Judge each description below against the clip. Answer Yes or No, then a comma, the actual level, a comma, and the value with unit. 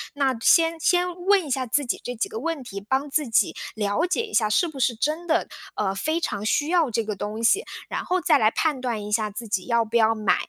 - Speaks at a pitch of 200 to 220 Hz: No, very high, 255 Hz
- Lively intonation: Yes, wide, 7.0 semitones